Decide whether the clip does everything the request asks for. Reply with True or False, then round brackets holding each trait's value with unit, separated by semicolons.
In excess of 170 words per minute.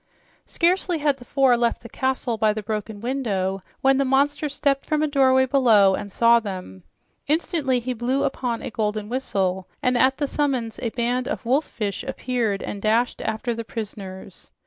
True (180 wpm)